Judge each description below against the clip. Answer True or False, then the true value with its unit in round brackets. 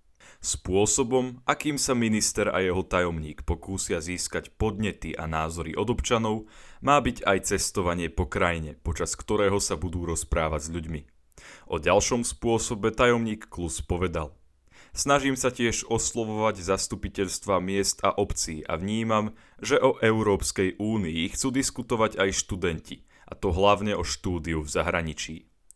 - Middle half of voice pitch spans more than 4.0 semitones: True (4.6 semitones)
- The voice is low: True (100 Hz)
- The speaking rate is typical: True (135 wpm)